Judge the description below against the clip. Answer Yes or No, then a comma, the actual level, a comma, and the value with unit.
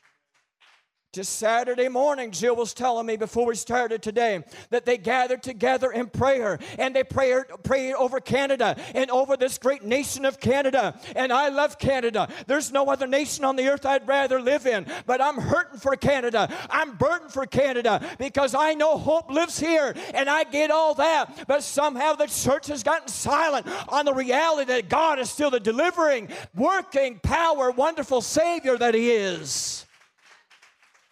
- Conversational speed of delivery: Yes, average, 170 wpm